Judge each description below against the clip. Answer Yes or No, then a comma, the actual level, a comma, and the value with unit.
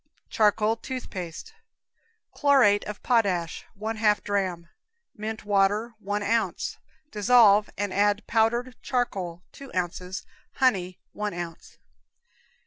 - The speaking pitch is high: Yes, high, 210 Hz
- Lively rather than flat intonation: No, average, 3.1 semitones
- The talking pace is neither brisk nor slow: No, slow, 105 wpm